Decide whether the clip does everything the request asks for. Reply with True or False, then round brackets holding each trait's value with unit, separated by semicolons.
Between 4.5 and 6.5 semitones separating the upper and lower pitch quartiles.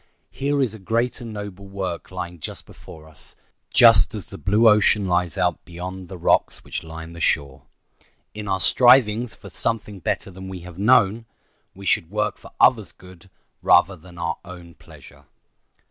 False (3.5 semitones)